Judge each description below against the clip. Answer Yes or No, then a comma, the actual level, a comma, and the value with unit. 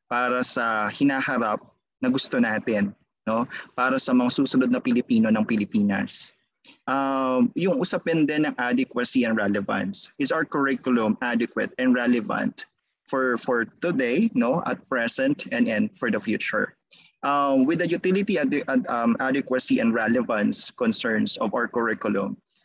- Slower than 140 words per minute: No, average, 145 wpm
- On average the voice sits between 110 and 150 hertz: Yes, medium, 140 Hz